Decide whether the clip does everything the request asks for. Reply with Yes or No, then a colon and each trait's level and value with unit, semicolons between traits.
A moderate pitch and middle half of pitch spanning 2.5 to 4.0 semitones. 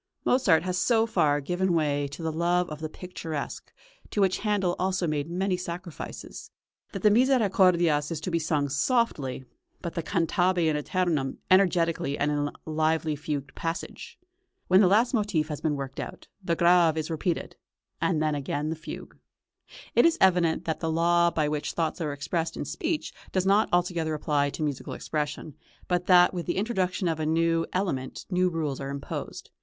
Yes: medium, 165 Hz; average, 3.2 semitones